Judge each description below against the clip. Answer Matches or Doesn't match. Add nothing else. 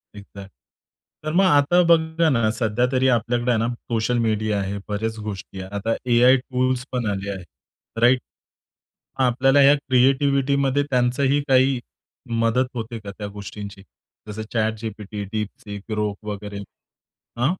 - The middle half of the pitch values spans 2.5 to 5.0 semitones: Matches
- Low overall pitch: Matches